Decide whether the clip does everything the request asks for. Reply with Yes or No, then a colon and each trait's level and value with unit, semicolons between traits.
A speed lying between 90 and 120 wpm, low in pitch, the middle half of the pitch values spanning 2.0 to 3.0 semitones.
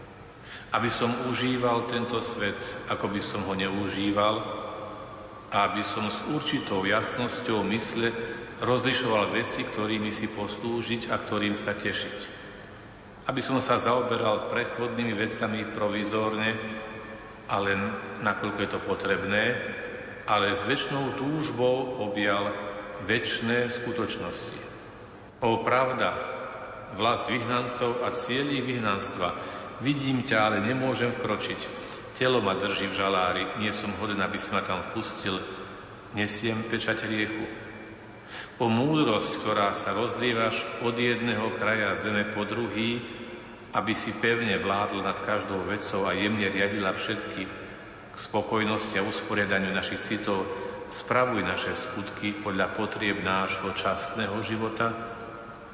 Yes: average, 115 wpm; low, 110 Hz; average, 2.7 semitones